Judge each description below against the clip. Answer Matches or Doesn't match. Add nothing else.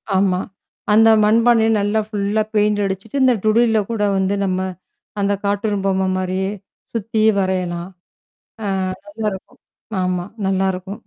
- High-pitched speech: Matches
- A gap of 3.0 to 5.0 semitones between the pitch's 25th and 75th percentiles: Doesn't match